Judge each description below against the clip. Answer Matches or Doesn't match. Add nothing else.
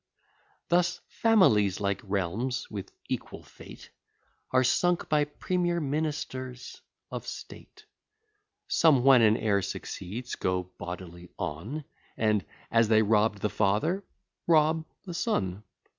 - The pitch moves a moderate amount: Doesn't match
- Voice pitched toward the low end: Matches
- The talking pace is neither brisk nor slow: Doesn't match